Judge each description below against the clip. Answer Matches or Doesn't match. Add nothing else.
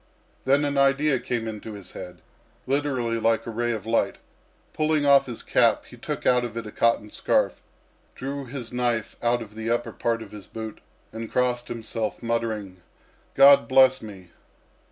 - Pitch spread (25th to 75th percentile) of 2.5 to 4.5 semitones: Matches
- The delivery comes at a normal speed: Matches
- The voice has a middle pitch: Doesn't match